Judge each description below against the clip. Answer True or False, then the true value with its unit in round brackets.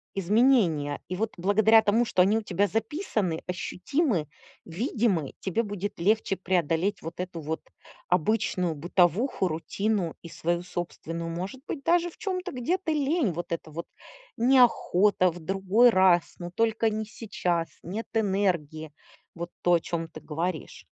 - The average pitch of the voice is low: False (190 Hz)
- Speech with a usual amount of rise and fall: True (4.7 semitones)